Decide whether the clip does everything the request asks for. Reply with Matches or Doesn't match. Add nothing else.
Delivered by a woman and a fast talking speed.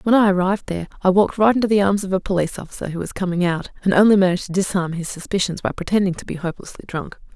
Matches